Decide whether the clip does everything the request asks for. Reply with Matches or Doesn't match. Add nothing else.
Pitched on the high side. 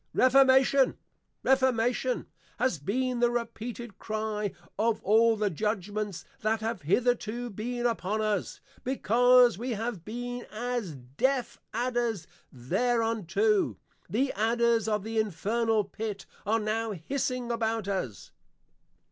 Matches